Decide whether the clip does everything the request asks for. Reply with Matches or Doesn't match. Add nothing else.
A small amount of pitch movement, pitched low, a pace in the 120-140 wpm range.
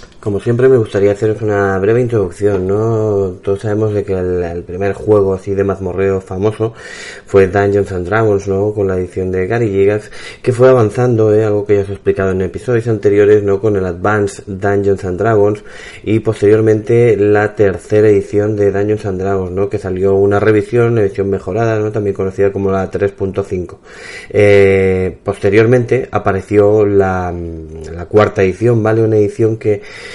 Doesn't match